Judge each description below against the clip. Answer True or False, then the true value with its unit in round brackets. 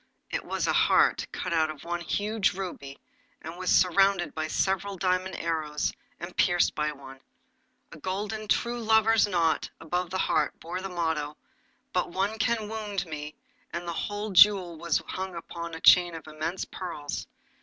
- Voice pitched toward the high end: False (175 Hz)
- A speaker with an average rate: True (165 wpm)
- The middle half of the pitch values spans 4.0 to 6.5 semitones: False (3.4 semitones)